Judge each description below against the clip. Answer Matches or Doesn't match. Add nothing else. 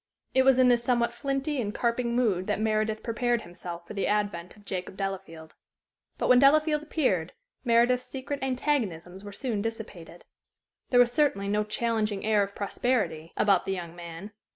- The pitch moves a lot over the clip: Doesn't match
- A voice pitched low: Doesn't match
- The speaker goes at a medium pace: Matches